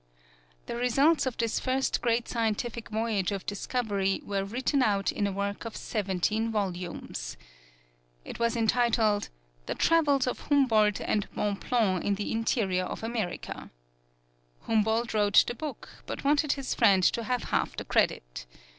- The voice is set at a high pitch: Yes, high, 220 Hz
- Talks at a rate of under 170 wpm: Yes, average, 145 wpm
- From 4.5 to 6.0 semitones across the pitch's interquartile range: No, average, 3.3 semitones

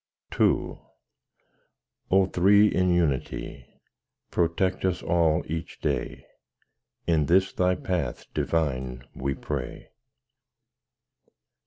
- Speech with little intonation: No, average, 3.6 semitones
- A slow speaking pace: Yes, slow, 95 wpm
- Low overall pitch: Yes, very low, 85 Hz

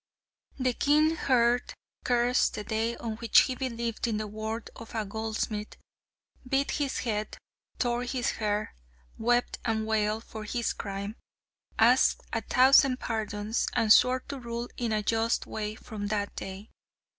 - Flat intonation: Yes, narrow, 2.3 semitones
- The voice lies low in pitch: No, high, 225 Hz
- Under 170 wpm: Yes, average, 150 wpm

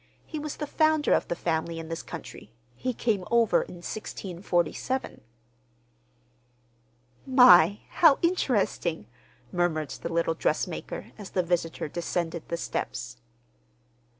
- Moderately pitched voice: Yes, medium, 175 Hz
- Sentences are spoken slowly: Yes, slow, 120 wpm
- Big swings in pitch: Yes, wide, 7.1 semitones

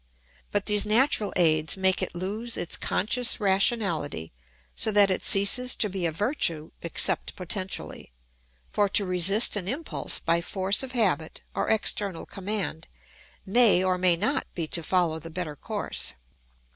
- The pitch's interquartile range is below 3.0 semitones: No, average, 3.7 semitones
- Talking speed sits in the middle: Yes, average, 150 wpm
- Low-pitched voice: No, high, 190 Hz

